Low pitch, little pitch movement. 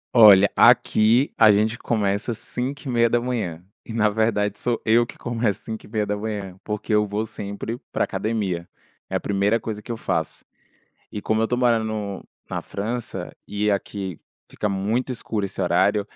Yes: low, 110 Hz; narrow, 2.2 semitones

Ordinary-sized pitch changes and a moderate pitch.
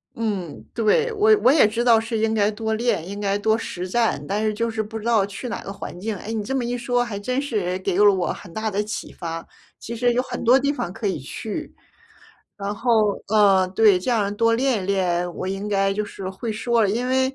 No: average, 3.2 semitones; high, 215 Hz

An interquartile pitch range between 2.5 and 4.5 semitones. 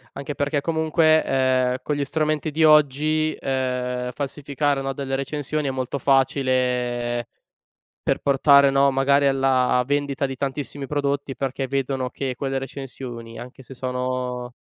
No: narrow, 1.9 semitones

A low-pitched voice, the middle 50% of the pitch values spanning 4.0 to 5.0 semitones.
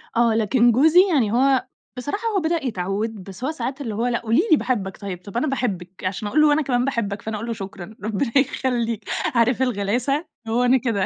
No: high, 235 Hz; average, 4.5 semitones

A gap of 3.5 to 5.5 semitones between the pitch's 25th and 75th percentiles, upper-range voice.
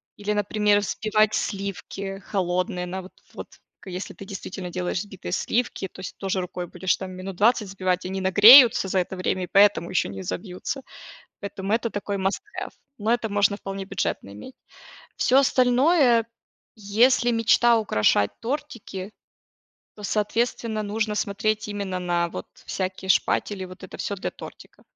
No: average, 2.8 semitones; high, 200 Hz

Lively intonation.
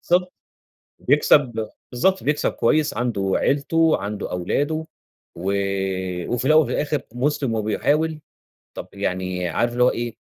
Yes: wide, 7.3 semitones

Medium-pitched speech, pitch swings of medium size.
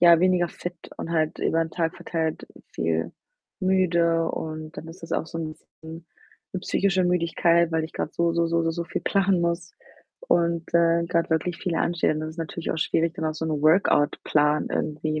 No: medium, 165 Hz; narrow, 1.3 semitones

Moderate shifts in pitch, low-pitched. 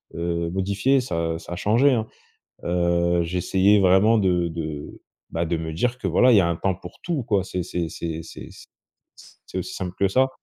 Yes: average, 3.6 semitones; very low, 90 Hz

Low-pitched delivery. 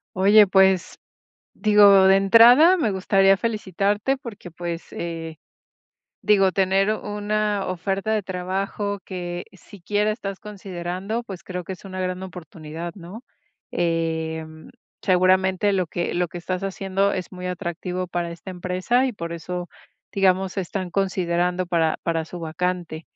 No: medium, 185 Hz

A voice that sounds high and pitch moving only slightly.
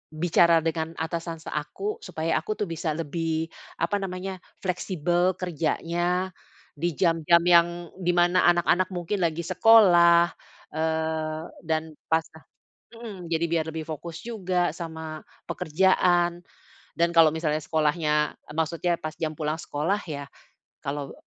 No: medium, 170 Hz; narrow, 1.9 semitones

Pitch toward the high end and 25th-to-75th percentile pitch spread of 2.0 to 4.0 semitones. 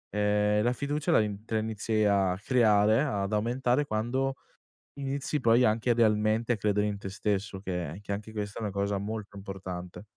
No: low, 105 Hz; narrow, 2.4 semitones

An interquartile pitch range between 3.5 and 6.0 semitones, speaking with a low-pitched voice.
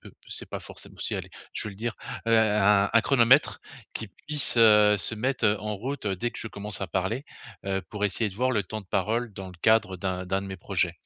No: average, 2.8 semitones; low, 105 Hz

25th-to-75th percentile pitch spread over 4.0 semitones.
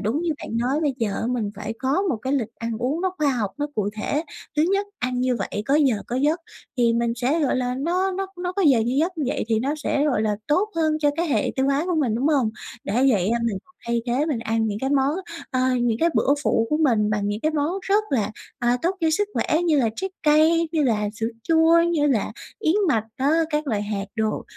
Yes: wide, 5.4 semitones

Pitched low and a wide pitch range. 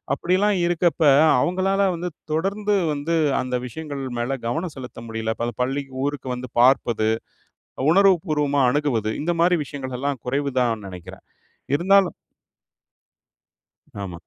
No: medium, 145 Hz; wide, 5.8 semitones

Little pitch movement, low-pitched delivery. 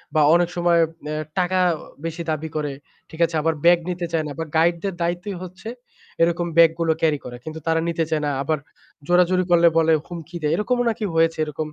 No: narrow, 1.7 semitones; medium, 165 Hz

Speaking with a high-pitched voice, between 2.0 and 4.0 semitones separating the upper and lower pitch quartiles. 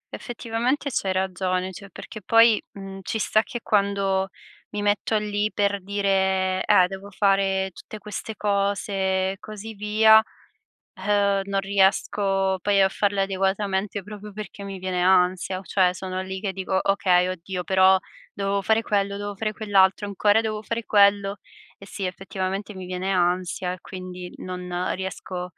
No: high, 195 Hz; narrow, 1.5 semitones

